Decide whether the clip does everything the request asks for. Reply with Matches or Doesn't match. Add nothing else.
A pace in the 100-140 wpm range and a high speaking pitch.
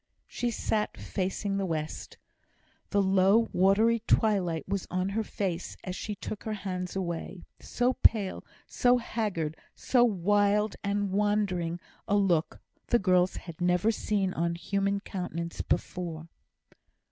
Matches